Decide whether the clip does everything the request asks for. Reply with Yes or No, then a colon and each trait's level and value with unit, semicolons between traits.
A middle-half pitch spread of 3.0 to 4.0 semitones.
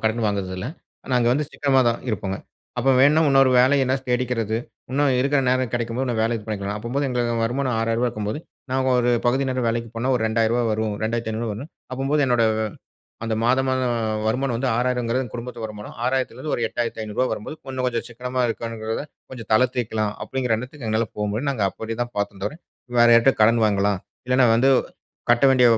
No: narrow, 2.6 semitones